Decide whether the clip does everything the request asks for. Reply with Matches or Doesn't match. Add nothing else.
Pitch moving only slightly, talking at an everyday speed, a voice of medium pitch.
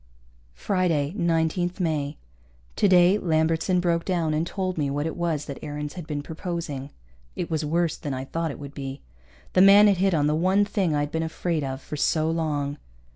Doesn't match